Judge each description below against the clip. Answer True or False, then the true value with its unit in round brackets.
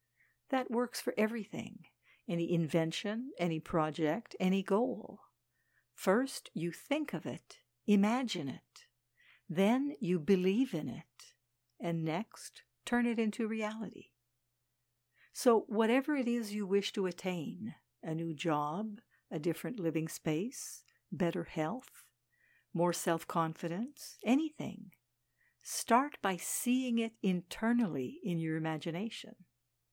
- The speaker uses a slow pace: True (115 wpm)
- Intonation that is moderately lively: False (5.9 semitones)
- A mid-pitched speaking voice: False (195 Hz)